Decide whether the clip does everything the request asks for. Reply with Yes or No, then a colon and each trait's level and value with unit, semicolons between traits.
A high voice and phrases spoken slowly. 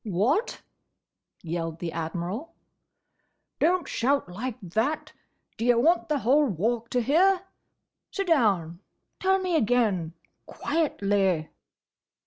Yes: high, 235 Hz; slow, 105 wpm